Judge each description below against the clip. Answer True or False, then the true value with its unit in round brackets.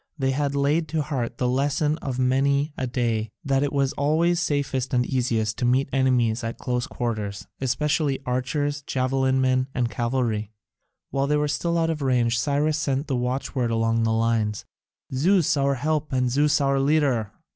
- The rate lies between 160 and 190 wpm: True (175 wpm)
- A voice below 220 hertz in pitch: True (135 Hz)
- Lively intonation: False (3.0 semitones)